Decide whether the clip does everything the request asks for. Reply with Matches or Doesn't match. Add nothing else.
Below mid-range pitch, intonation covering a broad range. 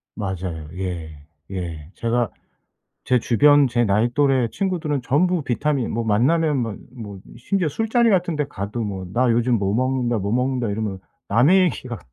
Matches